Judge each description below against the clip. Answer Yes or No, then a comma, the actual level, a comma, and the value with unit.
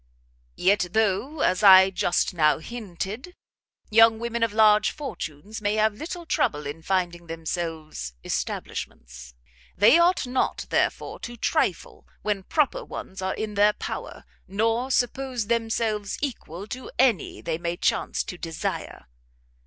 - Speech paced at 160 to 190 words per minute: No, slow, 135 wpm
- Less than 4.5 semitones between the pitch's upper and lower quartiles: No, average, 5.2 semitones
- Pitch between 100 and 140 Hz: No, high, 210 Hz